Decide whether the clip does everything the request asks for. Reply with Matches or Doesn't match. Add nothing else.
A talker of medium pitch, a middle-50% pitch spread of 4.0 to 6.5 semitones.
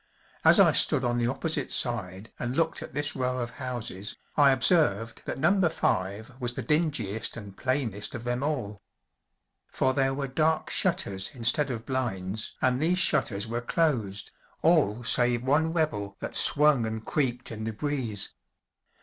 Doesn't match